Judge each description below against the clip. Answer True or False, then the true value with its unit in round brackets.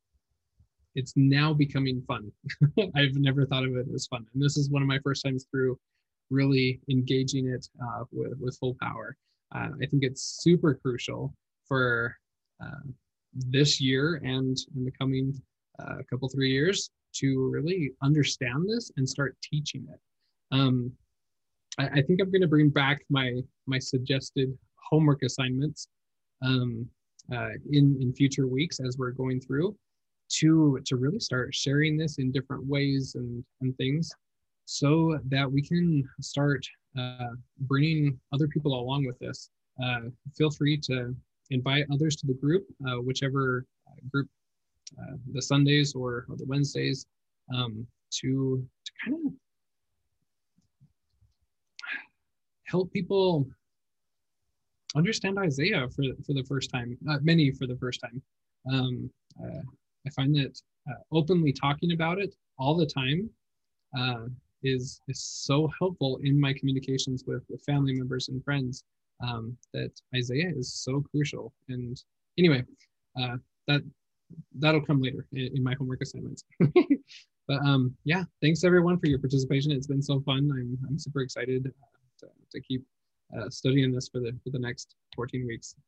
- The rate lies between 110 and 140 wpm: False (150 wpm)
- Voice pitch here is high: False (135 Hz)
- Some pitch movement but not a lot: False (2.3 semitones)